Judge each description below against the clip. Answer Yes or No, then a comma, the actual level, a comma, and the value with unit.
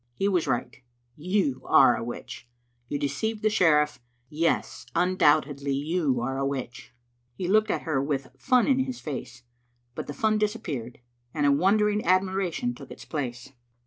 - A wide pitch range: Yes, wide, 6.7 semitones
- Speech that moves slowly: No, average, 165 wpm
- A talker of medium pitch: Yes, medium, 155 Hz